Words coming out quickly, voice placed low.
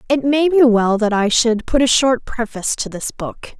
No: fast, 235 wpm; high, 240 Hz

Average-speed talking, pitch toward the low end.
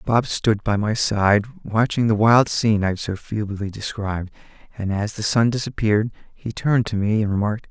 Yes: average, 195 wpm; low, 105 Hz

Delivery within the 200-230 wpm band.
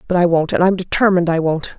No: fast, 270 wpm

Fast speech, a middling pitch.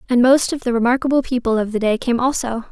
No: fast, 245 wpm; high, 245 Hz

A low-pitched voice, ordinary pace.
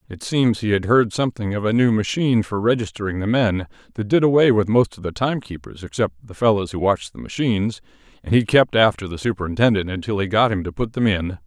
No: low, 105 Hz; fast, 225 wpm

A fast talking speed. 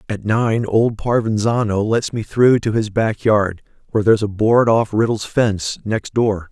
No: average, 185 wpm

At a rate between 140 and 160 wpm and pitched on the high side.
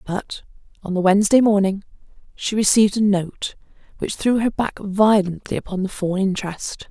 Yes: average, 155 wpm; high, 200 Hz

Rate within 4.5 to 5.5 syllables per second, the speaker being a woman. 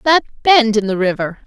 Yes: 5.2 syllables/s; female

